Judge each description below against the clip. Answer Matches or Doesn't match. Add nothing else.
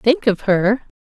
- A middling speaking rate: Matches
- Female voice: Matches